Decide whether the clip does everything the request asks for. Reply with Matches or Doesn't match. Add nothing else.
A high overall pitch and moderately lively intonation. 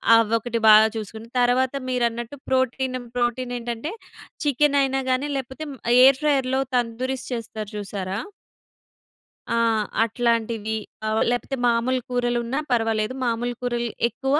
Doesn't match